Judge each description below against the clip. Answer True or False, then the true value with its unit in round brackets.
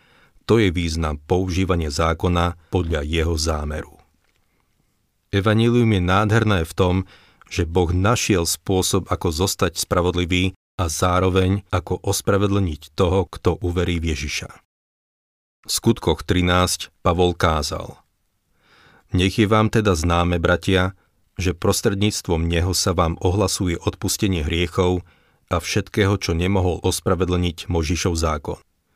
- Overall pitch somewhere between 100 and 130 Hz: False (90 Hz)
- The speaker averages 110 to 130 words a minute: True (115 wpm)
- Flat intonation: True (2.3 semitones)